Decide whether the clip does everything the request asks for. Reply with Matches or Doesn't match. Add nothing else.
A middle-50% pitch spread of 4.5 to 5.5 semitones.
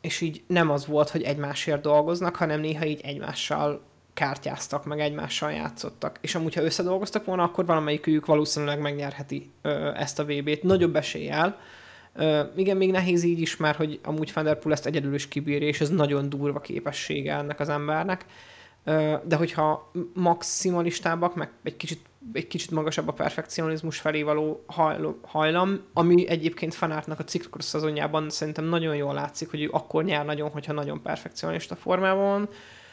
Doesn't match